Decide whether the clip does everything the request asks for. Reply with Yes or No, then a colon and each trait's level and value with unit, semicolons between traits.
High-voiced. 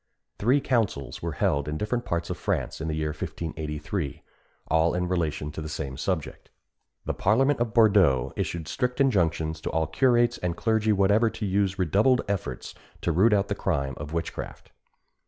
No: very low, 90 Hz